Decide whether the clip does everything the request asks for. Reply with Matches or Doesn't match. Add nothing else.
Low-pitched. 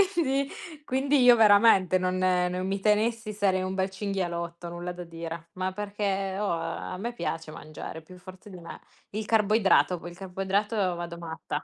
Doesn't match